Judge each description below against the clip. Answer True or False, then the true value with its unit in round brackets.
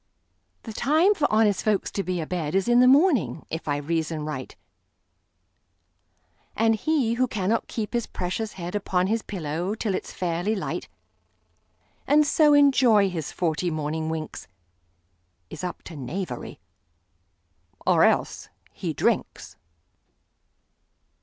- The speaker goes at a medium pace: False (120 wpm)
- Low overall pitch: False (185 Hz)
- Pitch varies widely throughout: True (6.3 semitones)